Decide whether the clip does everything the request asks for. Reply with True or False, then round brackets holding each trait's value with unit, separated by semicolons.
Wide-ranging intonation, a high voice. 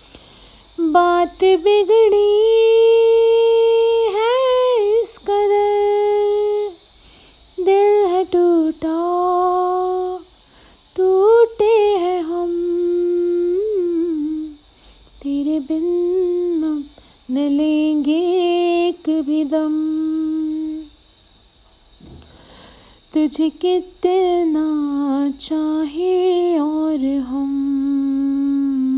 False (4.7 semitones; 350 Hz)